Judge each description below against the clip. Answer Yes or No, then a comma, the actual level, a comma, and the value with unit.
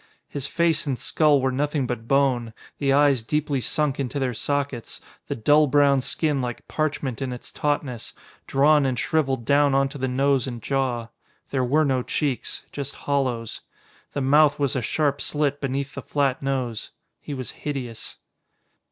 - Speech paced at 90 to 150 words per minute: No, average, 165 wpm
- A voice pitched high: No, low, 135 Hz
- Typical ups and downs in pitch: No, narrow, 2.3 semitones